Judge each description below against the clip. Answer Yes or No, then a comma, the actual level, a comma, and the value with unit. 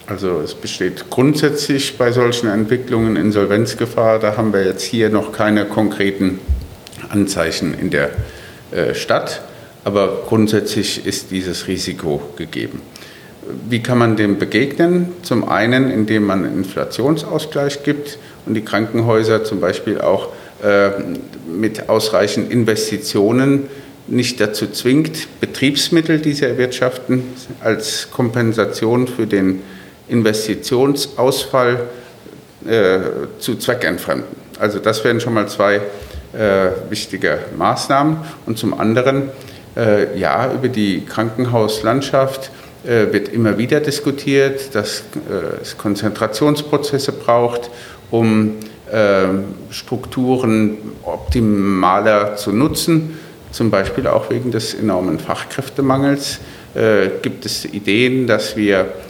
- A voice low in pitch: Yes, low, 115 Hz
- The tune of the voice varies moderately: Yes, average, 4.6 semitones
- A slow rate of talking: Yes, slow, 110 wpm